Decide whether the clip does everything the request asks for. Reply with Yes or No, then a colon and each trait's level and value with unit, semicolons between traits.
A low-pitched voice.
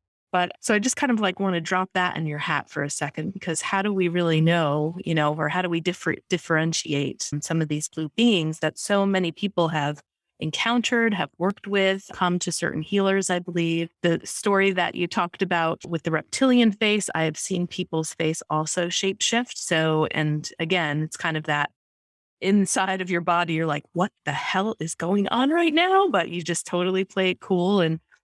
No: medium, 175 Hz